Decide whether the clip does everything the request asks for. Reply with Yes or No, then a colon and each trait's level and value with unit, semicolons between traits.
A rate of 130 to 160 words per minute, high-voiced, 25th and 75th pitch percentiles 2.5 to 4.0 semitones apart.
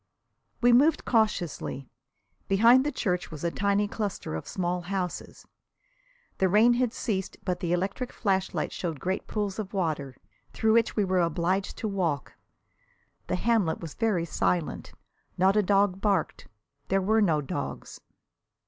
Yes: average, 150 wpm; high, 195 Hz; average, 3.6 semitones